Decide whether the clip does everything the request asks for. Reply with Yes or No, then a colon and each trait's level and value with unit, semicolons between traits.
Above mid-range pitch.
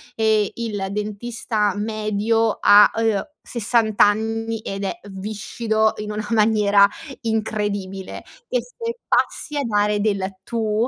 Yes: high, 215 Hz